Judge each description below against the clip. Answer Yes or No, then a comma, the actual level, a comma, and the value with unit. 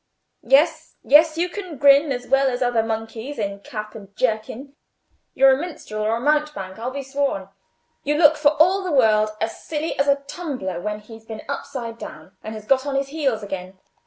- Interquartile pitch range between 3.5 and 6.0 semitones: Yes, average, 5.1 semitones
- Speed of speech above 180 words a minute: Yes, average, 195 wpm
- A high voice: Yes, very high, 260 Hz